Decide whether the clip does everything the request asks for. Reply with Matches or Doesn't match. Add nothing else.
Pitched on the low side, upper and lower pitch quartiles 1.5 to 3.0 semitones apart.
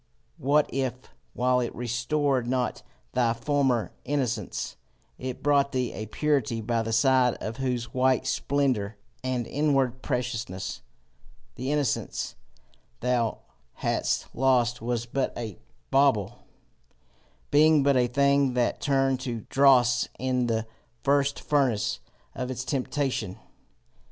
Matches